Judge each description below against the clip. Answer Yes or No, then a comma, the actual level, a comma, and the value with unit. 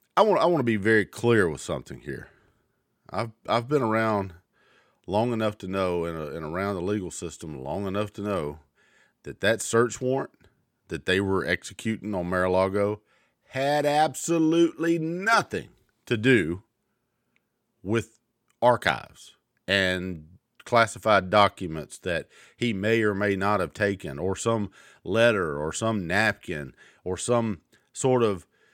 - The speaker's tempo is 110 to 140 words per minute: Yes, slow, 135 wpm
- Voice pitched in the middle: No, low, 105 Hz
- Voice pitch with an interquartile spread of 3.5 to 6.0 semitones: Yes, average, 3.8 semitones